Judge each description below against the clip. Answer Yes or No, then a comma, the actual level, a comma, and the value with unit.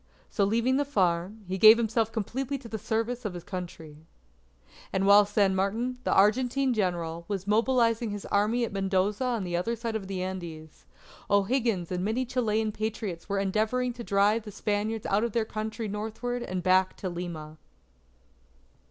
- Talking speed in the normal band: Yes, average, 170 wpm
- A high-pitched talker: Yes, high, 210 Hz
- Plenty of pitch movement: No, average, 3.5 semitones